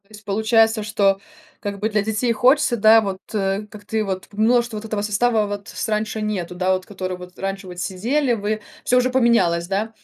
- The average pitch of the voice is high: Yes, high, 210 Hz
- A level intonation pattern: Yes, narrow, 2.3 semitones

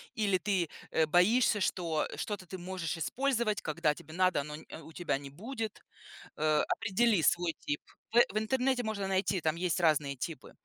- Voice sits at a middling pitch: Yes, medium, 180 Hz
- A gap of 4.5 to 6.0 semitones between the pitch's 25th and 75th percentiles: Yes, average, 5.2 semitones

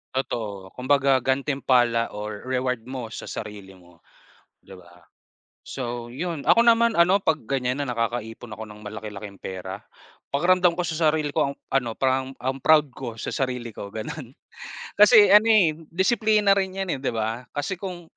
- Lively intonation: Yes, wide, 6.7 semitones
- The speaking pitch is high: No, low, 130 Hz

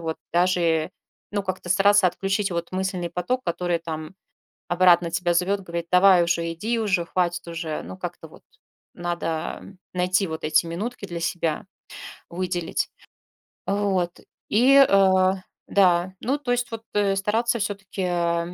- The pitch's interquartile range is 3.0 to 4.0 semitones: No, narrow, 2.5 semitones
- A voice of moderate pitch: Yes, medium, 180 Hz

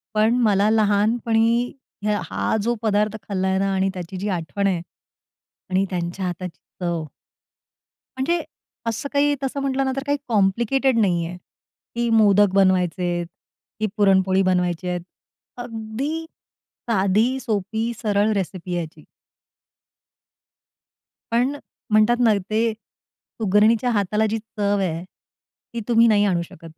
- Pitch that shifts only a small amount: No, average, 3.6 semitones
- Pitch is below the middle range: No, high, 210 Hz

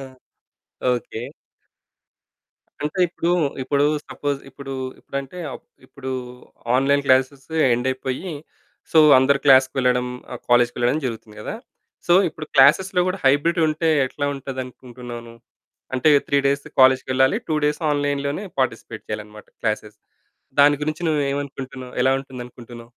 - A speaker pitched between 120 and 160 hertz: Yes, low, 135 Hz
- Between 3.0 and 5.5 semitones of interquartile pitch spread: No, narrow, 2.5 semitones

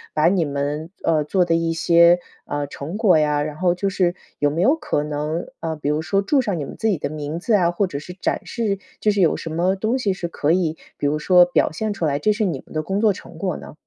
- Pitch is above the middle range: No, medium, 170 Hz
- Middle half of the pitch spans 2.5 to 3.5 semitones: No, average, 4.3 semitones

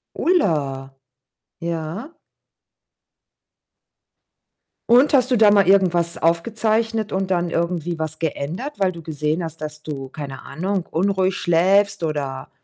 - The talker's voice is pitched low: No, medium, 170 Hz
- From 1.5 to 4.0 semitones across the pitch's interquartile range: No, average, 4.4 semitones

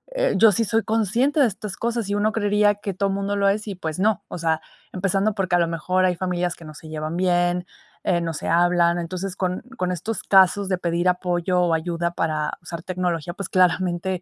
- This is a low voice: No, medium, 180 Hz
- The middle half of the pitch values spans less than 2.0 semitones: No, narrow, 2.6 semitones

